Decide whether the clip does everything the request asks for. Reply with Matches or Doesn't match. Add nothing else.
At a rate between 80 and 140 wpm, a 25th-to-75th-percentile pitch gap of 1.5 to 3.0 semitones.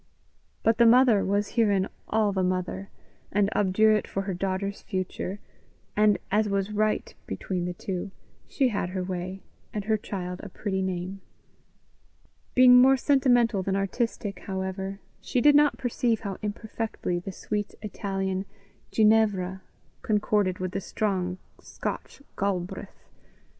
Matches